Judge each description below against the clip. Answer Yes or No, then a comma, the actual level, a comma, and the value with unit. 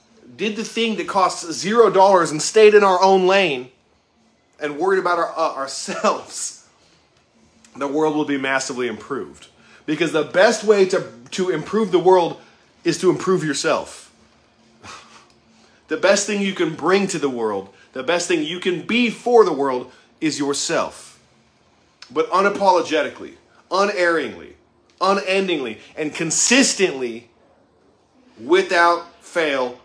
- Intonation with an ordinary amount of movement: Yes, average, 4.1 semitones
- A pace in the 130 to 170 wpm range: Yes, slow, 135 wpm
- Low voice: No, medium, 175 Hz